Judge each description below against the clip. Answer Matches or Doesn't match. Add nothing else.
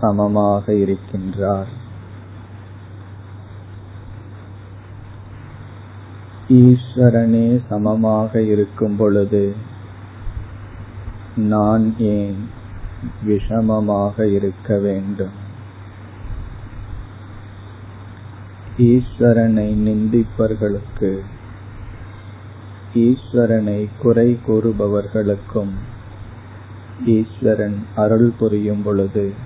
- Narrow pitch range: Matches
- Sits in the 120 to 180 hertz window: Doesn't match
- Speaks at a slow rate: Matches